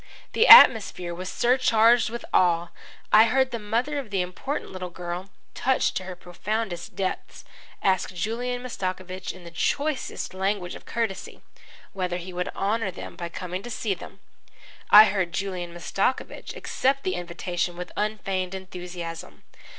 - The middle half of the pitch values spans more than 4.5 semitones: No, average, 4.0 semitones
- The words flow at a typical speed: Yes, average, 150 wpm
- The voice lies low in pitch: No, high, 190 Hz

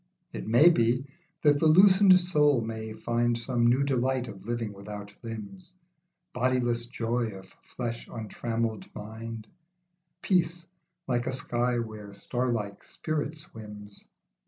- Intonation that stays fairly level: No, average, 3.7 semitones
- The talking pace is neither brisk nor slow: No, slow, 125 wpm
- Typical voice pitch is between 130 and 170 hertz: No, low, 120 Hz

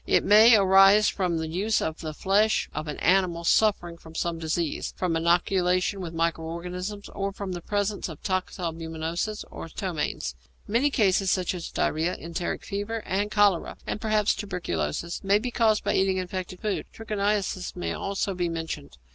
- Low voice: No, medium, 185 Hz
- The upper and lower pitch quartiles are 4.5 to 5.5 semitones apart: No, average, 3.4 semitones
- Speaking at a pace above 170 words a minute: No, average, 165 wpm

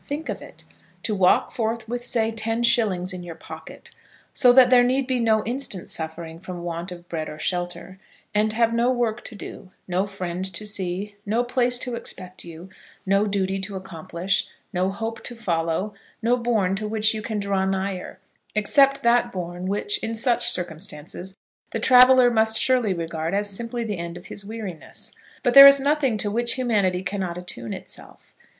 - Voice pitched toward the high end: Yes, high, 205 Hz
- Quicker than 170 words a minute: Yes, average, 185 wpm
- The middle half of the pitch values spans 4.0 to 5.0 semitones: Yes, average, 4.5 semitones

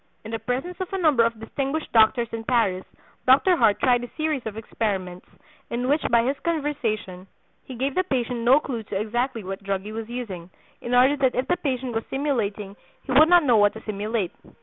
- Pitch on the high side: Yes, high, 240 Hz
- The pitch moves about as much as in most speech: Yes, average, 4.2 semitones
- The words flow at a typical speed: No, fast, 210 wpm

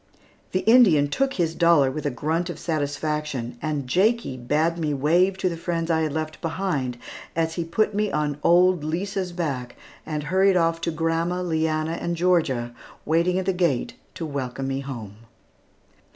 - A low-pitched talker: No, medium, 165 Hz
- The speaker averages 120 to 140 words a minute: No, average, 170 wpm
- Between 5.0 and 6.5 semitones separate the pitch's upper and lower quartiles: No, average, 3.3 semitones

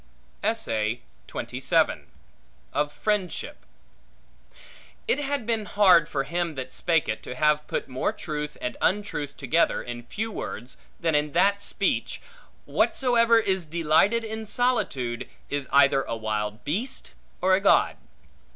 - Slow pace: Yes, slow, 125 wpm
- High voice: No, medium, 165 Hz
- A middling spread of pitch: No, wide, 7.0 semitones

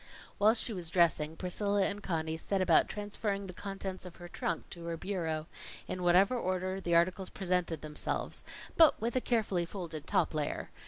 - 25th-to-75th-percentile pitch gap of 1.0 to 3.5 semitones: Yes, average, 3.0 semitones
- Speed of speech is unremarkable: Yes, average, 175 wpm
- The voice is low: No, medium, 185 Hz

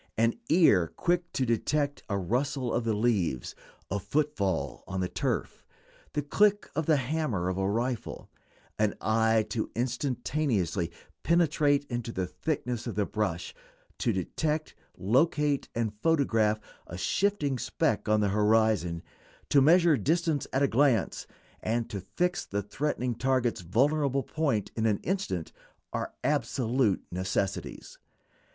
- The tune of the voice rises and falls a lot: Yes, wide, 6.2 semitones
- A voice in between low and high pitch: No, low, 120 Hz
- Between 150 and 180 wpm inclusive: No, slow, 135 wpm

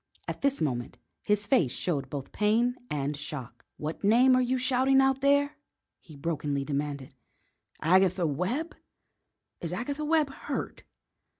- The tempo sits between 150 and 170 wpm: No, slow, 135 wpm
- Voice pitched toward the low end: No, high, 190 Hz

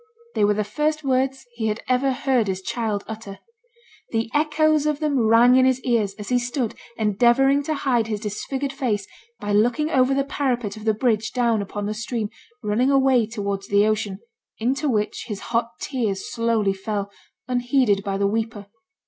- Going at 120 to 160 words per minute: No, average, 180 wpm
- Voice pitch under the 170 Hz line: No, high, 230 Hz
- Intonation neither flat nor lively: Yes, average, 4.0 semitones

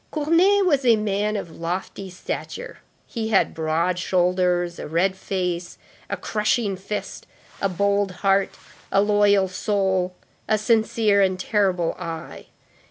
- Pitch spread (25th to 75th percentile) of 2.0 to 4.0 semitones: Yes, average, 2.7 semitones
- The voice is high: Yes, high, 195 Hz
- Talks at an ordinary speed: No, slow, 130 wpm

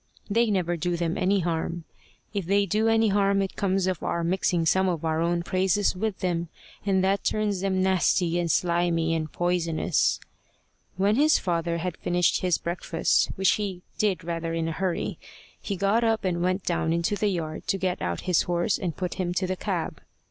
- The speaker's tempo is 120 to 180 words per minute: No, average, 195 wpm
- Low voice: No, medium, 180 Hz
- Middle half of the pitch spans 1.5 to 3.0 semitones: Yes, narrow, 2.4 semitones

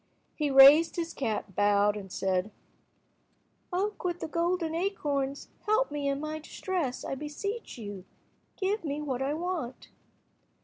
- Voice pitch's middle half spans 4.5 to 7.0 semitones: Yes, wide, 5.4 semitones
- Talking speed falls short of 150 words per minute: Yes, average, 140 wpm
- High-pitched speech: Yes, very high, 295 Hz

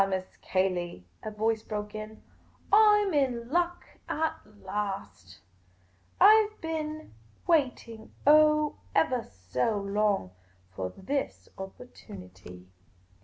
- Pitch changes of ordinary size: No, wide, 8.5 semitones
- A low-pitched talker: No, high, 220 Hz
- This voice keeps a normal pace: No, slow, 105 wpm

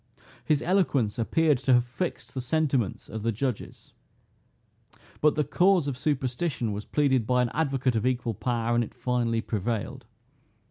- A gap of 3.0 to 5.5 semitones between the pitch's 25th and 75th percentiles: Yes, average, 3.7 semitones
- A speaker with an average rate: Yes, average, 155 wpm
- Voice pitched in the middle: No, low, 125 Hz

